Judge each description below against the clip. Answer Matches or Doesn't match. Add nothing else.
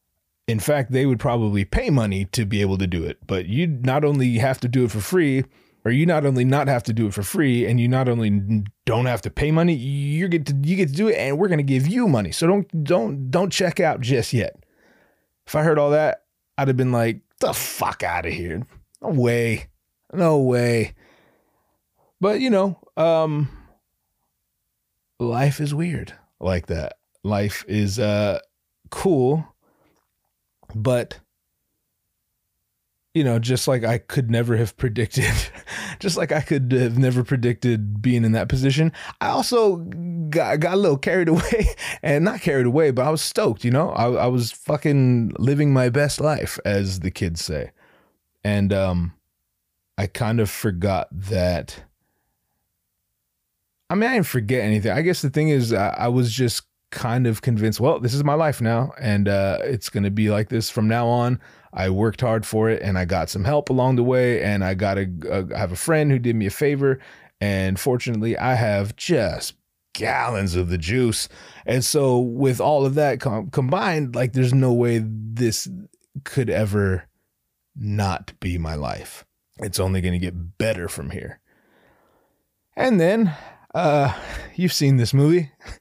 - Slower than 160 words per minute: Doesn't match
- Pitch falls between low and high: Doesn't match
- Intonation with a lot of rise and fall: Matches